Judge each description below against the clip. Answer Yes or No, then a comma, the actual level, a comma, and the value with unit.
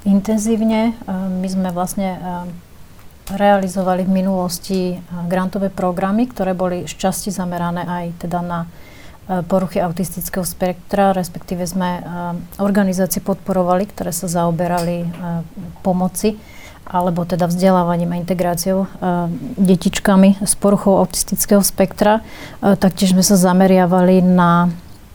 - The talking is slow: Yes, slow, 105 wpm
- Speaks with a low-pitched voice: No, medium, 185 Hz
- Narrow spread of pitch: Yes, narrow, 1.8 semitones